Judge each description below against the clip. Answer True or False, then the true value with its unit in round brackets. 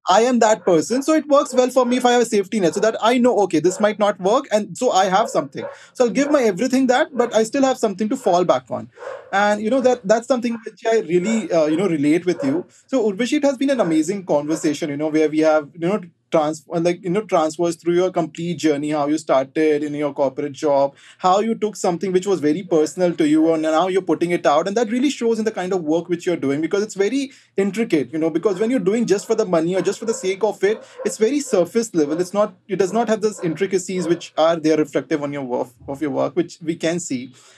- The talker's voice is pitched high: True (195 Hz)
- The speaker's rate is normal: False (265 wpm)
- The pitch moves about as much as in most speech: False (6.0 semitones)